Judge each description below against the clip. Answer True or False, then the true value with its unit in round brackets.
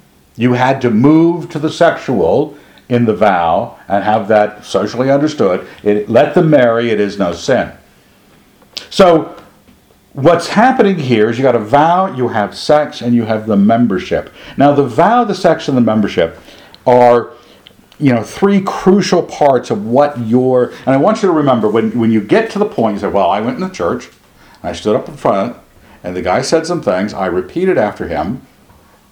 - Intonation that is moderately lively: False (7.0 semitones)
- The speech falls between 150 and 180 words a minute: False (190 wpm)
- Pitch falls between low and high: False (125 Hz)